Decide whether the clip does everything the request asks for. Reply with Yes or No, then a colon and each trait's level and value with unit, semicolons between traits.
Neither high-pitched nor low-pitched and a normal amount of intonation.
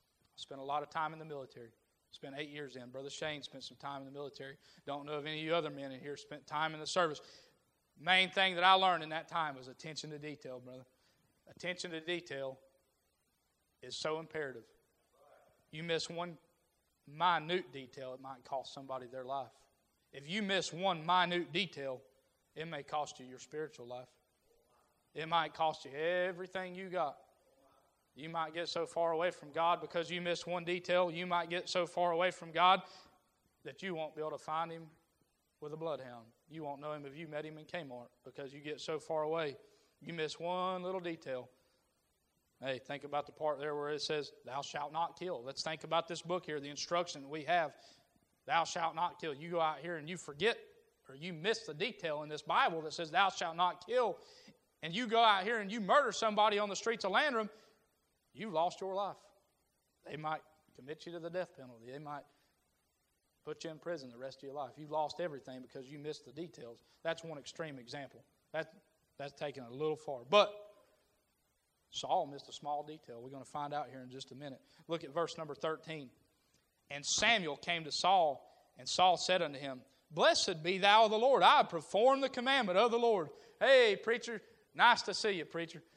Yes: medium, 155 Hz; average, 4.1 semitones